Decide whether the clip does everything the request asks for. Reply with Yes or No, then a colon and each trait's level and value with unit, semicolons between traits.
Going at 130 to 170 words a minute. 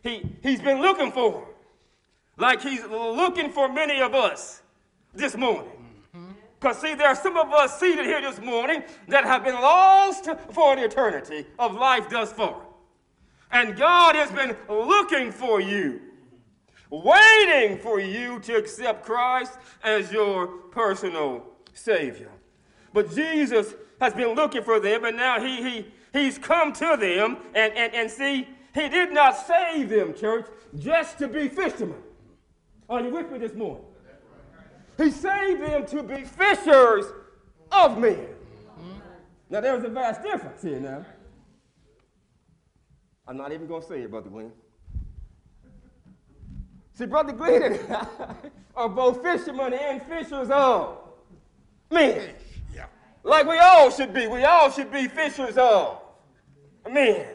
Yes: average, 140 wpm